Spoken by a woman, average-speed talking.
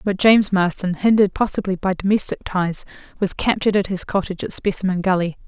Yes: female; average, 175 wpm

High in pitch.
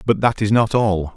No: low, 105 Hz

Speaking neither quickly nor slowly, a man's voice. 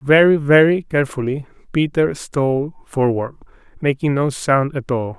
No: slow, 125 wpm; male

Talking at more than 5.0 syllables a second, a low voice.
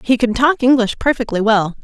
No: 5.4 syllables/s; high, 235 Hz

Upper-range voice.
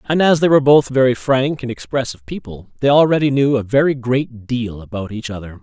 No: low, 125 Hz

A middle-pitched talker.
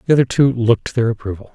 No: low, 120 Hz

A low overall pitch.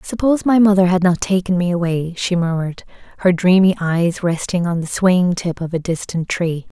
No: medium, 180 Hz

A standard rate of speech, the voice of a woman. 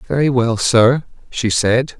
No: average, 150 wpm; male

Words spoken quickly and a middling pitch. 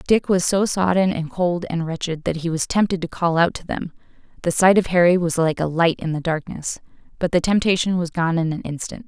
Yes: fast, 225 wpm; medium, 170 Hz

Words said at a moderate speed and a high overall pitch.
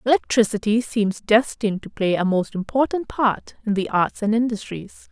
Yes: average, 165 wpm; high, 220 Hz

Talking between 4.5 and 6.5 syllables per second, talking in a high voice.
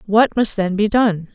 No: 4.2 syllables/s; high, 210 Hz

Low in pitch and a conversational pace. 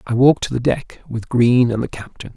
No: low, 120 Hz; fast, 230 wpm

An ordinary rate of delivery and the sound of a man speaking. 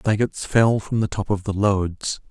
No: fast, 235 wpm; male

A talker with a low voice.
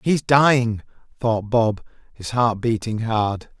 Yes: low, 115 Hz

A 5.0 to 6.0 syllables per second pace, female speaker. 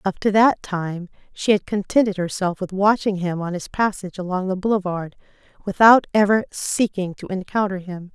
Yes: 5.1 syllables/s; female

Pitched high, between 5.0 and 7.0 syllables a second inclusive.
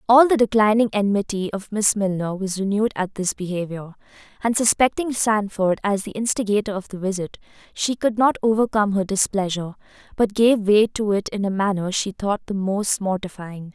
Yes: high, 205 Hz; 5.4 syllables/s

